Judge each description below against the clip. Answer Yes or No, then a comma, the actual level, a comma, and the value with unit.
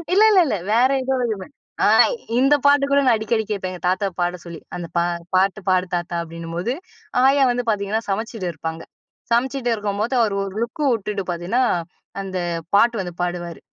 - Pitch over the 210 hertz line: No, high, 205 Hz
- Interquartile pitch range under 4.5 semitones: No, average, 5.2 semitones